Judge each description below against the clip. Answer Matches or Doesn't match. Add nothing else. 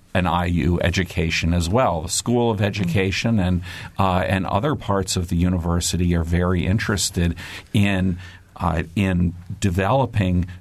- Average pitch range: Doesn't match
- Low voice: Matches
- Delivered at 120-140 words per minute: Matches